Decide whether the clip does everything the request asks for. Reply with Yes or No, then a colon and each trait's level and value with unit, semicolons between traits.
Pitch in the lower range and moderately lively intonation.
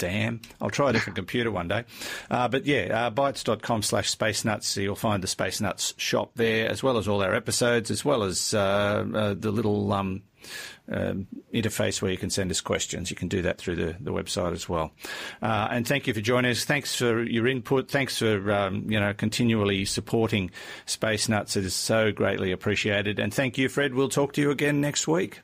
Yes: low, 110 Hz; average, 3.1 semitones